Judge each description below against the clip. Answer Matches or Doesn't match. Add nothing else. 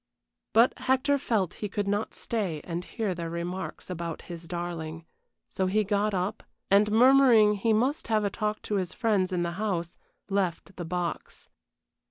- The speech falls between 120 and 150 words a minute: Doesn't match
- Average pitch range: Matches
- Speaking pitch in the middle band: Doesn't match